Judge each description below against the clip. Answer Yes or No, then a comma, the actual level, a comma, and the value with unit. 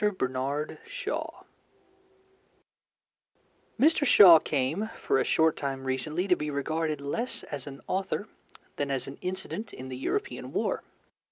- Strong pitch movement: Yes, wide, 5.8 semitones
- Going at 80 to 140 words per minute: Yes, slow, 135 wpm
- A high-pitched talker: No, medium, 150 Hz